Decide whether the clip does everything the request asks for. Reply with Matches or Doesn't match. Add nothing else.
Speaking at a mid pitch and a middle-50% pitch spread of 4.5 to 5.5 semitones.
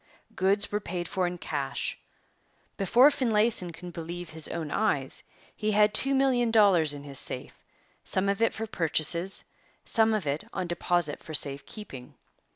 Matches